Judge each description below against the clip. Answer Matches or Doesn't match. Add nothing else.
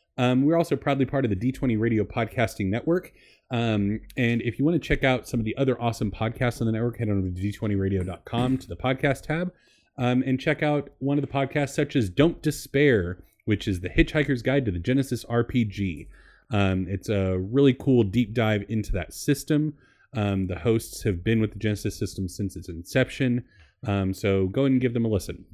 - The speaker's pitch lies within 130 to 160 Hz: Doesn't match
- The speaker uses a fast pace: Matches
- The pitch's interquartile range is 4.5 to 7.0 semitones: Matches